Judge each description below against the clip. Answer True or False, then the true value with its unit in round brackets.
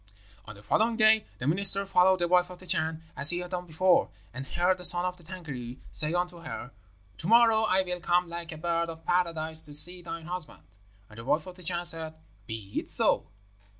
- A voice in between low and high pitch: True (175 Hz)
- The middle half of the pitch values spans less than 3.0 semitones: True (2.4 semitones)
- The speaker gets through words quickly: True (220 wpm)